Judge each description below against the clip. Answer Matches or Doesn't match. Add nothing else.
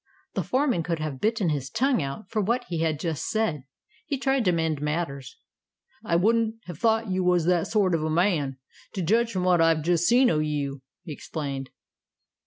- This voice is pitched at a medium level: Matches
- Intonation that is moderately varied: Doesn't match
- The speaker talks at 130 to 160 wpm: Doesn't match